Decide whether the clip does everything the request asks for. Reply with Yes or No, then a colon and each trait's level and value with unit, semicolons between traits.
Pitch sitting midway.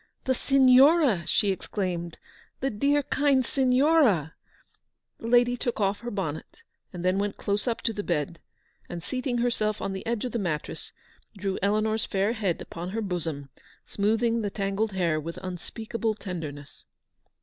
No: high, 205 Hz